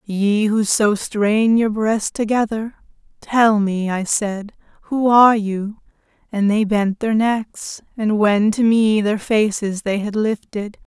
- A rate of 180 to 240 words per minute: No, average, 155 wpm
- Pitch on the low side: No, high, 215 Hz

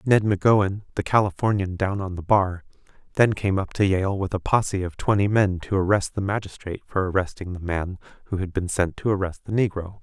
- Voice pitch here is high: No, very low, 95 Hz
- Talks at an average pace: No, fast, 210 wpm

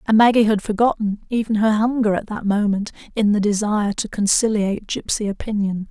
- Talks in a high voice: Yes, high, 210 Hz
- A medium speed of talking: Yes, average, 175 wpm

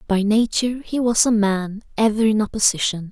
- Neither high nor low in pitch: No, high, 215 Hz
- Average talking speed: Yes, average, 175 wpm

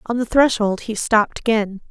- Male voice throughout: No, female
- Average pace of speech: Yes, average, 190 wpm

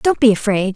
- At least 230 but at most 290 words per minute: Yes, fast, 240 wpm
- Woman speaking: Yes, female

